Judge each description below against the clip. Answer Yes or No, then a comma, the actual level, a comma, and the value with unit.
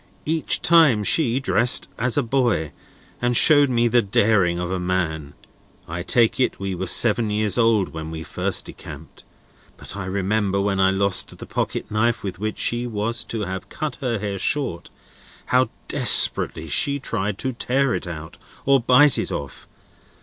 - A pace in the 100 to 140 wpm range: No, average, 170 wpm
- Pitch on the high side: No, low, 105 Hz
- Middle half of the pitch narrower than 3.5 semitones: No, average, 4.6 semitones